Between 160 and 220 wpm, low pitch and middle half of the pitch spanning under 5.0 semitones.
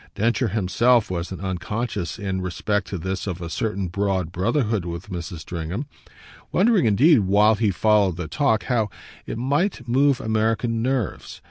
No: average, 150 wpm; low, 105 Hz; average, 4.2 semitones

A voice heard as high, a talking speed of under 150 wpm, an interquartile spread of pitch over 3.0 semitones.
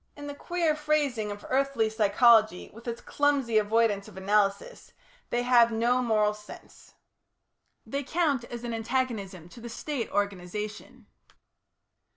Yes: high, 230 Hz; slow, 135 wpm; average, 4.1 semitones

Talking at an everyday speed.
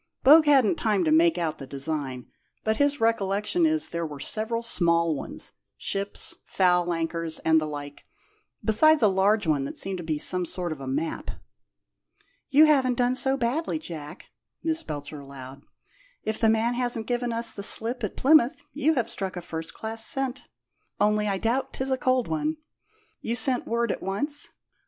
Yes: average, 180 wpm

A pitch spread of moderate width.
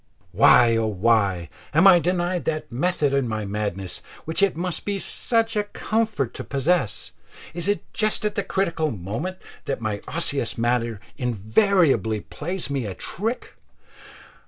No: wide, 8.7 semitones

